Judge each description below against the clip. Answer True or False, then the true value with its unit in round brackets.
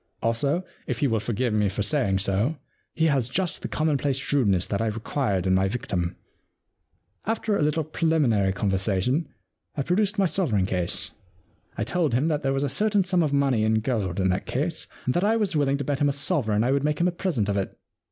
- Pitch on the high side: False (135 Hz)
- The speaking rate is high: True (220 wpm)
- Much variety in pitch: True (7.2 semitones)